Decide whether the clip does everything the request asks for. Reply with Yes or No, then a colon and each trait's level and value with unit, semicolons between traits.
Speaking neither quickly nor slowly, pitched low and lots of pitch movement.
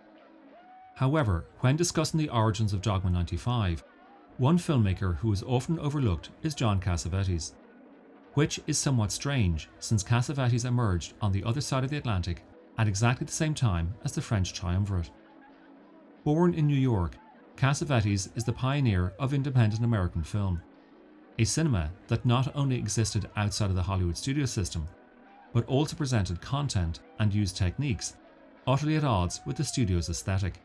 Yes: average, 155 wpm; low, 115 Hz; wide, 6.6 semitones